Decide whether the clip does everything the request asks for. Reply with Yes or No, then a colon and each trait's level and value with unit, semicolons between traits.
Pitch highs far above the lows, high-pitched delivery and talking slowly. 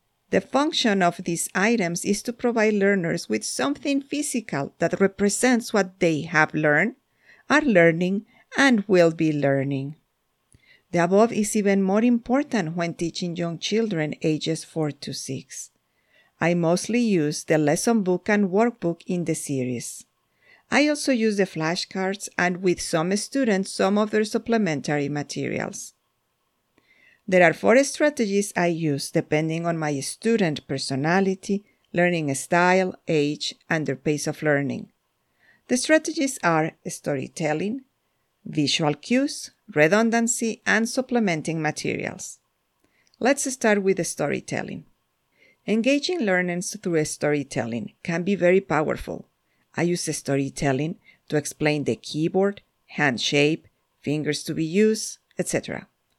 No: wide, 6.0 semitones; medium, 180 Hz; slow, 130 wpm